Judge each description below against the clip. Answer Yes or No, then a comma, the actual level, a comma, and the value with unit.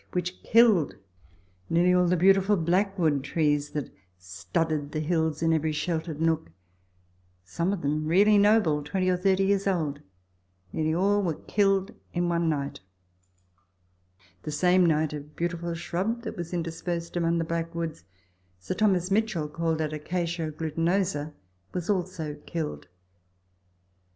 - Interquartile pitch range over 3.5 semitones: No, average, 3.1 semitones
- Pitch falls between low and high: Yes, medium, 170 Hz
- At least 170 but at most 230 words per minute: No, slow, 135 wpm